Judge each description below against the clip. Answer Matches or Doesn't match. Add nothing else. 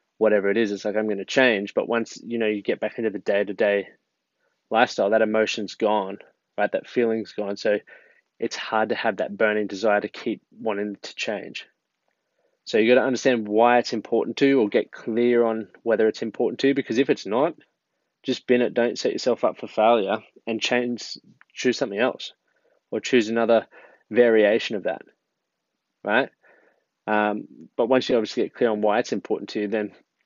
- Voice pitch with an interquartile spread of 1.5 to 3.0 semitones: Matches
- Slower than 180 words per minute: Doesn't match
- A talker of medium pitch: Doesn't match